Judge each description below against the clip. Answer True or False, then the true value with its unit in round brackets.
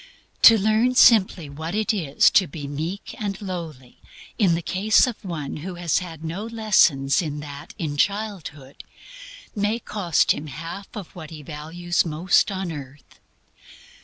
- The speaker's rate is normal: True (155 wpm)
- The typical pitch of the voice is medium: True (170 Hz)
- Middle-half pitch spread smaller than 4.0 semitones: False (5.1 semitones)